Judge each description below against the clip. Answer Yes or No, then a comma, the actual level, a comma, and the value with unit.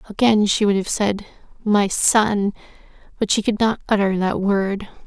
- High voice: Yes, high, 205 Hz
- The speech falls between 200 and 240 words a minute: No, average, 165 wpm